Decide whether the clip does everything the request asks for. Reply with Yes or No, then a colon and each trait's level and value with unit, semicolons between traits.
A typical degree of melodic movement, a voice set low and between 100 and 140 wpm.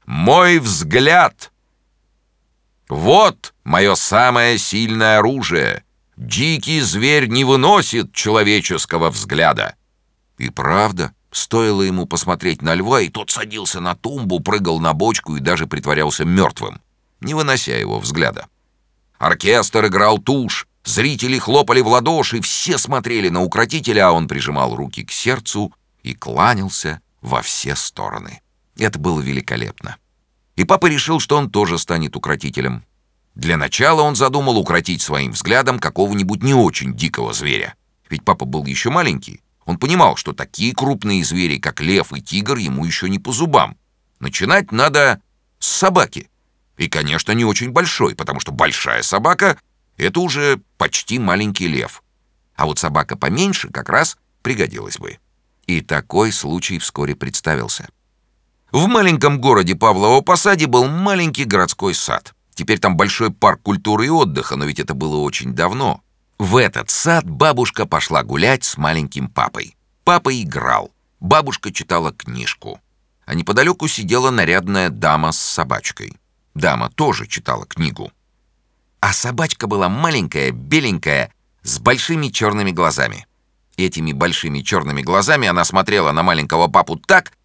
No: wide, 9.0 semitones; low, 105 Hz; average, 135 wpm